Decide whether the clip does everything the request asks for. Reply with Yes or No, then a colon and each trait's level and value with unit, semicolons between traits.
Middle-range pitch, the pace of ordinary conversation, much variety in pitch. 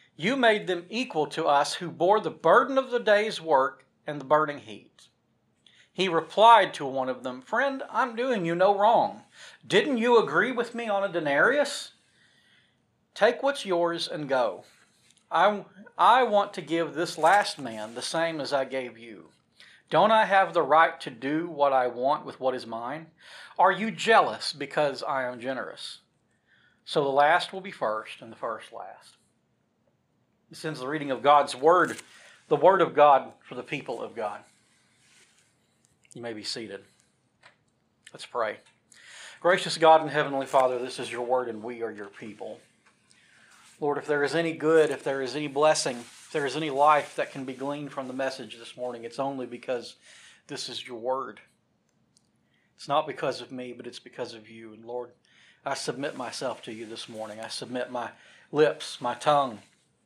Yes: medium, 145 Hz; average, 180 wpm; wide, 5.7 semitones